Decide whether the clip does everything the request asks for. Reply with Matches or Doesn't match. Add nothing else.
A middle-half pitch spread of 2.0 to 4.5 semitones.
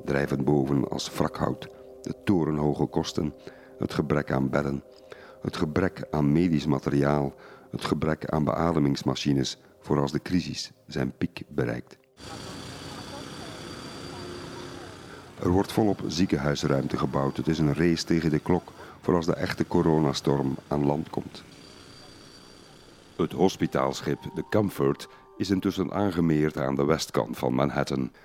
Matches